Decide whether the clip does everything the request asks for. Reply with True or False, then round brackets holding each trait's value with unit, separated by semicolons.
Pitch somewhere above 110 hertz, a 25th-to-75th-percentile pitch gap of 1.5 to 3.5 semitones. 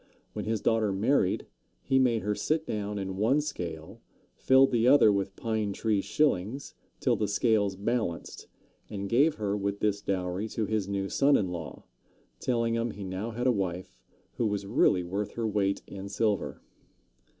False (105 Hz; 3.1 semitones)